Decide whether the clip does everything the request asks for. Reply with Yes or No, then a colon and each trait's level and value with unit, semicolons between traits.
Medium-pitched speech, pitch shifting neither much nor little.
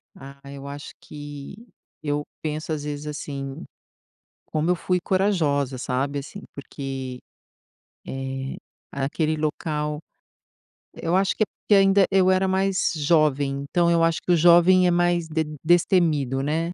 Yes: medium, 155 Hz; average, 3.7 semitones